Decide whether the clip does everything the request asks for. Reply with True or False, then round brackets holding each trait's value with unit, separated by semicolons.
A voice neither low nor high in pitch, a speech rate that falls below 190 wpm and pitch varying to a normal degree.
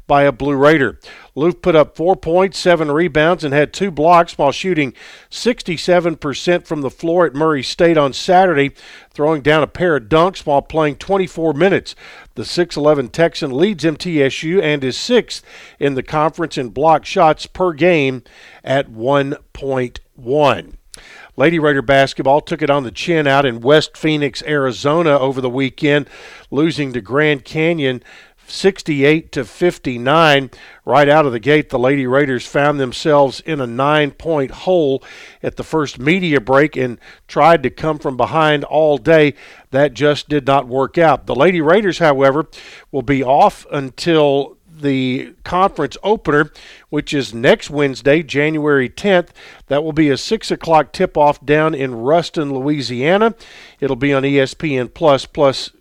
True (150 Hz; 155 wpm; 3.1 semitones)